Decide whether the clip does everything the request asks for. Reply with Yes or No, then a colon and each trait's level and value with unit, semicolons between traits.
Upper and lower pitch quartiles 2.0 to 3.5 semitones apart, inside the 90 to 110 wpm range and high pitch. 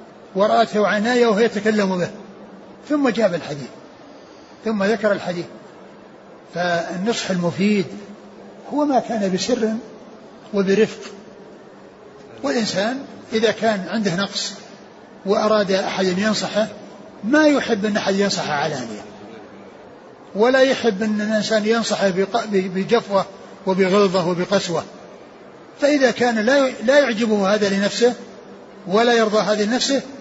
Yes: narrow, 2.6 semitones; average, 100 wpm; high, 215 Hz